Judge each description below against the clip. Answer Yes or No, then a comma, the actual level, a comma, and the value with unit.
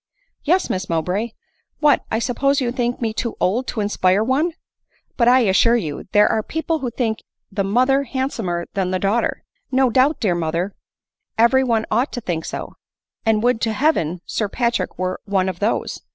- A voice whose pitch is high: Yes, high, 225 Hz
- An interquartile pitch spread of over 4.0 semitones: Yes, average, 5.2 semitones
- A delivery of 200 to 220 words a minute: Yes, fast, 205 wpm